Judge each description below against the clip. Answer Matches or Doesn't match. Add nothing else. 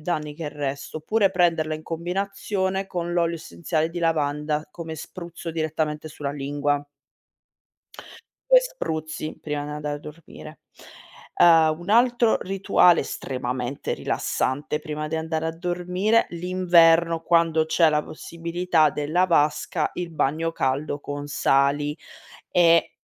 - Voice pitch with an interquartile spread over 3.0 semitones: Doesn't match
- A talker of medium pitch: Matches